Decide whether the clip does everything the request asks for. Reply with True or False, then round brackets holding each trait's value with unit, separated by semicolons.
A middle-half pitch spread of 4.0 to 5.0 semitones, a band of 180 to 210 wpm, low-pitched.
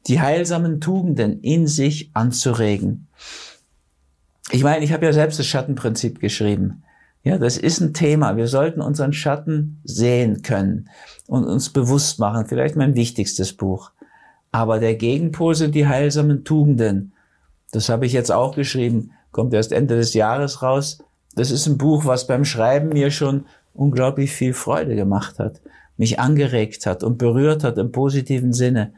False (4.7 semitones; 155 wpm; 130 Hz)